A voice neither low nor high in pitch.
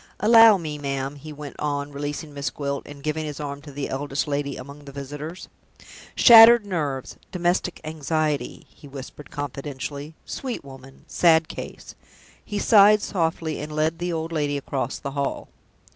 Yes: medium, 150 Hz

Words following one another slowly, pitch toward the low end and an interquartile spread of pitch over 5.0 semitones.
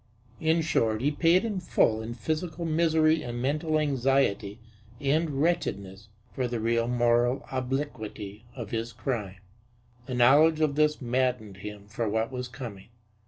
No: average, 145 wpm; low, 125 Hz; wide, 5.4 semitones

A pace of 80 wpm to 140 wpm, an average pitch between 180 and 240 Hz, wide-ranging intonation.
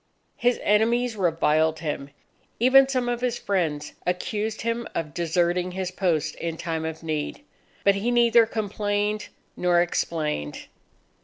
Yes: slow, 135 wpm; medium, 185 Hz; wide, 5.9 semitones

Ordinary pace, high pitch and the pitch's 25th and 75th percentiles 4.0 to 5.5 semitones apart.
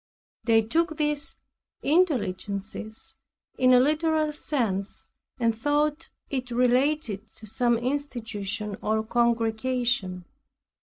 No: slow, 95 wpm; high, 240 Hz; average, 5.0 semitones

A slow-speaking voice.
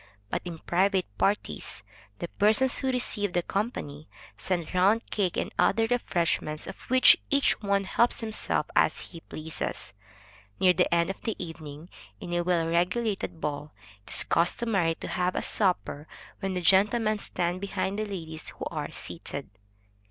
No: average, 160 wpm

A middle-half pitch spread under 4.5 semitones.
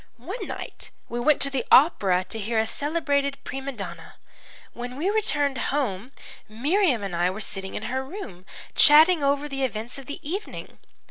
No: average, 5.2 semitones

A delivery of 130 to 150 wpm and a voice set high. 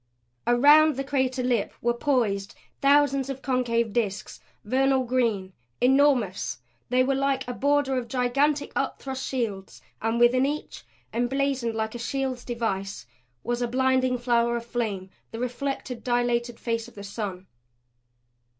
Yes: average, 140 wpm; high, 245 Hz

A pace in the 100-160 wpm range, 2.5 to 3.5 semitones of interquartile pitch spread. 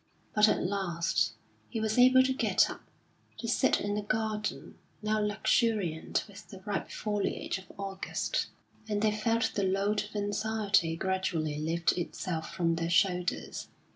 Yes: average, 150 wpm; average, 3.1 semitones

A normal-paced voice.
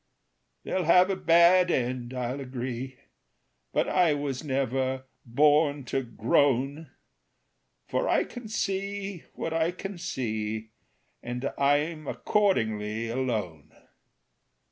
No: slow, 105 wpm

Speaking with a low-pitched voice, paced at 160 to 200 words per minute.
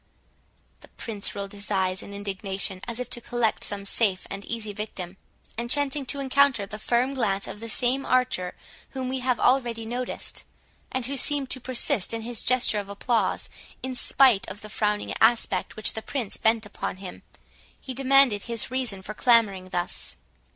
No: high, 230 Hz; average, 180 wpm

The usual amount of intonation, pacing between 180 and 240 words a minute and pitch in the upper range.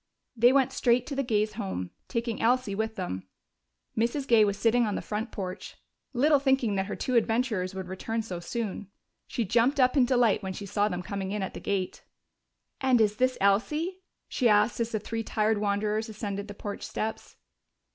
Yes: average, 3.3 semitones; average, 195 wpm; high, 220 Hz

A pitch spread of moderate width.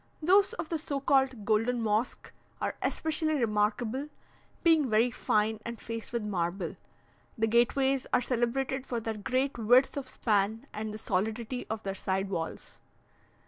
Yes: average, 3.9 semitones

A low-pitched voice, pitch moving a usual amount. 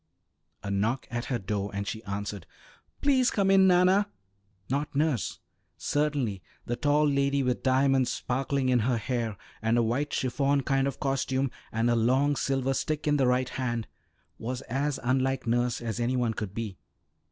Yes: low, 130 Hz; average, 3.1 semitones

